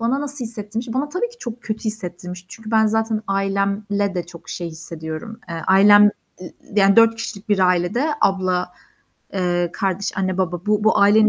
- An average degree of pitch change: Yes, average, 3.4 semitones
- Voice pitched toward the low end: No, high, 200 Hz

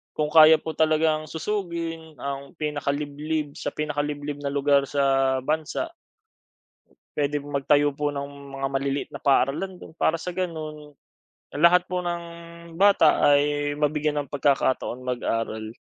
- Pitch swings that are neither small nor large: No, narrow, 2.2 semitones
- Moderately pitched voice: Yes, medium, 150 Hz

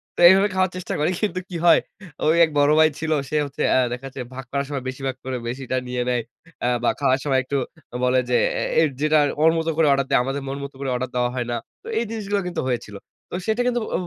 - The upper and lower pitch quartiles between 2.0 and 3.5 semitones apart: No, average, 4.1 semitones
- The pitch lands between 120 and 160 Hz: Yes, medium, 140 Hz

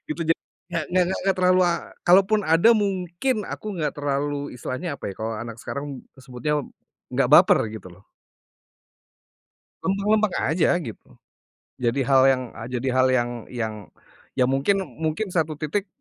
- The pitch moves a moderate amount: No, wide, 6.1 semitones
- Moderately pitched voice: Yes, medium, 155 Hz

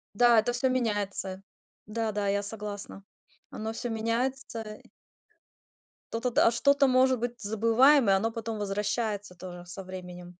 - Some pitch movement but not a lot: Yes, average, 3.3 semitones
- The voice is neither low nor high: No, high, 220 Hz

